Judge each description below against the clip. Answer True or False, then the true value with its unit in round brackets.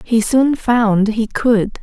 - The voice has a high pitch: True (225 Hz)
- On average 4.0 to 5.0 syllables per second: False (3.1 syllables/s)